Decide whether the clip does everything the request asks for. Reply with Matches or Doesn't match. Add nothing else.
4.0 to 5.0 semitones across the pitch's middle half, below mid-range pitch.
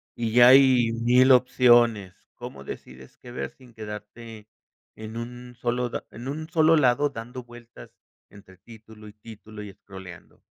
Doesn't match